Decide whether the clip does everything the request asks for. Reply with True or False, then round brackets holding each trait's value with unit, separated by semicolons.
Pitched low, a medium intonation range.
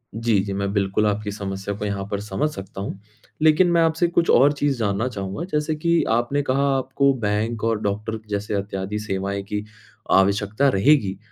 False (105 Hz; 5.8 semitones)